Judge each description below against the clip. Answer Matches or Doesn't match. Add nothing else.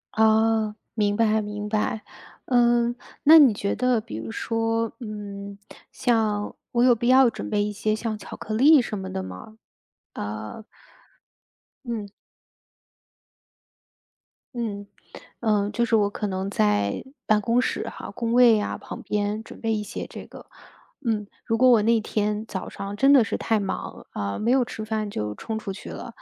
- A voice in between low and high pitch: Doesn't match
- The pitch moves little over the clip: Matches